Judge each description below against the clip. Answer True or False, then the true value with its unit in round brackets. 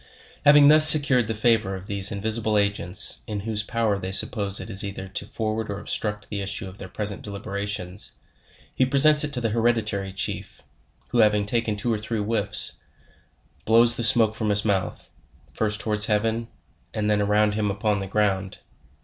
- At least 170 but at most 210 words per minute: True (185 wpm)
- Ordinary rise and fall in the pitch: False (2.0 semitones)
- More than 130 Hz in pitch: False (105 Hz)